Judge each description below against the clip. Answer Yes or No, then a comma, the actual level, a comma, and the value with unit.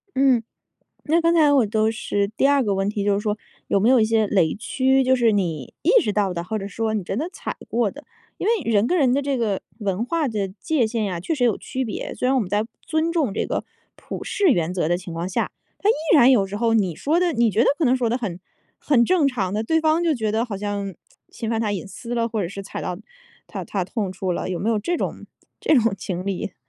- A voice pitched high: Yes, high, 220 Hz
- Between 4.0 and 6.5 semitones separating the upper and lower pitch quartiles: Yes, average, 4.8 semitones